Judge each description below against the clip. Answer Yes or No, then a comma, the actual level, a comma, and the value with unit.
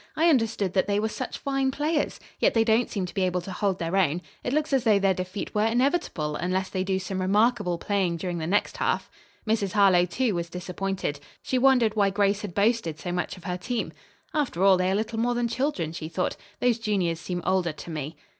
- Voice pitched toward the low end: No, high, 195 Hz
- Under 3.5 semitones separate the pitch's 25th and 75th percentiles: No, average, 4.3 semitones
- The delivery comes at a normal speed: No, fast, 225 wpm